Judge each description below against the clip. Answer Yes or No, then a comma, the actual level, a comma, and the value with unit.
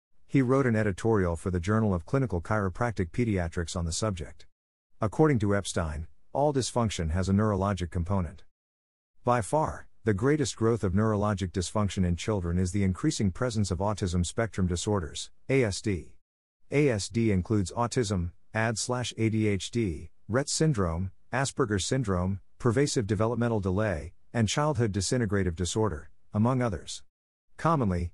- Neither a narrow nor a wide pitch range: Yes, average, 4.7 semitones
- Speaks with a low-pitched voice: Yes, low, 105 Hz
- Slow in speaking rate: Yes, slow, 130 wpm